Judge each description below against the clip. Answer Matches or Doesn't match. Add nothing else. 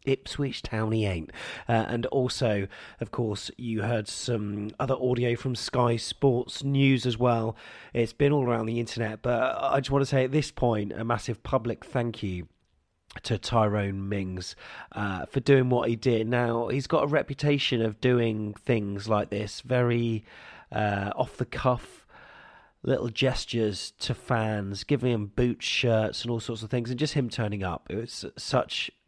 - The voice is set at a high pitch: Doesn't match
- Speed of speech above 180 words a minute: Doesn't match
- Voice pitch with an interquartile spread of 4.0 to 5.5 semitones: Doesn't match